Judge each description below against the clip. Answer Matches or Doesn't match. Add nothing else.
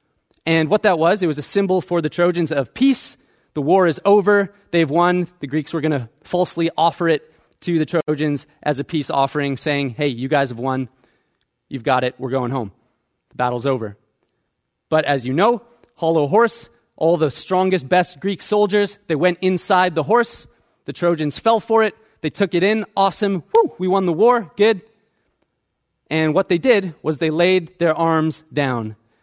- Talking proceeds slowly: Doesn't match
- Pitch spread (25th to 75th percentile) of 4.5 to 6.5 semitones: Matches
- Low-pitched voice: Doesn't match